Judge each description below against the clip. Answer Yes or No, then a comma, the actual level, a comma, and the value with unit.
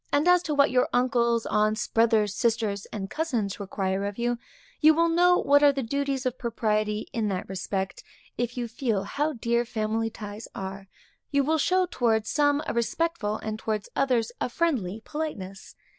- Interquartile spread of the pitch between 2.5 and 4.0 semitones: No, average, 5.0 semitones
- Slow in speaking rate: No, average, 175 wpm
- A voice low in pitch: No, high, 235 Hz